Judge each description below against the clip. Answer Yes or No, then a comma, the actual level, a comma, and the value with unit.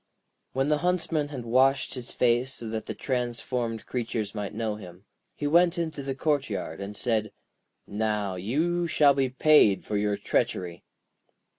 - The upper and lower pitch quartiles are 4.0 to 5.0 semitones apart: No, wide, 5.4 semitones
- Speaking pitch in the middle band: No, low, 120 Hz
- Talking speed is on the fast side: No, average, 160 wpm